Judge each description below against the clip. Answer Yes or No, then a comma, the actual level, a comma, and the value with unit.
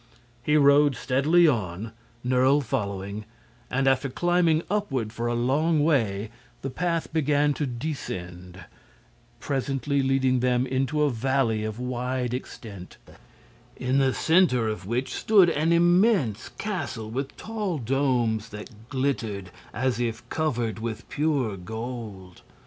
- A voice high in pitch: No, low, 130 Hz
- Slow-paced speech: Yes, slow, 125 wpm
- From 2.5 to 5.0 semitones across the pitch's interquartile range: Yes, average, 4.6 semitones